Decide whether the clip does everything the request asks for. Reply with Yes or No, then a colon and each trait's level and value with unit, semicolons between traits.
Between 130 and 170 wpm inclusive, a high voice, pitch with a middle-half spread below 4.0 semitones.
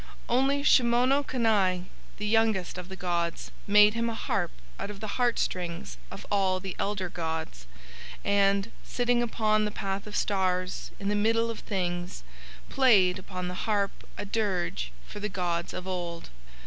Yes: average, 160 wpm; high, 200 Hz; average, 3.5 semitones